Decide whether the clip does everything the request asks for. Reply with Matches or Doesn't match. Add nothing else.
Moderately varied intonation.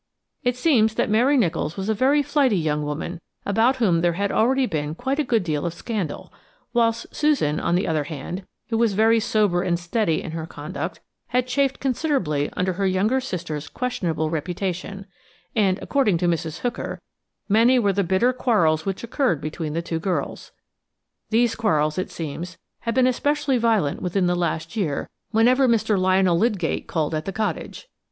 Doesn't match